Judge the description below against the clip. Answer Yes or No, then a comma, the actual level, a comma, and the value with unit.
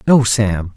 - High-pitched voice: No, low, 110 Hz